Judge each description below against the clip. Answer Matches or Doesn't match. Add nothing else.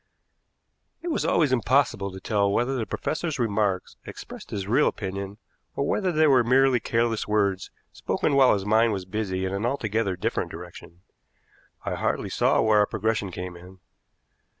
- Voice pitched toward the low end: Matches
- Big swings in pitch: Doesn't match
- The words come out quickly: Doesn't match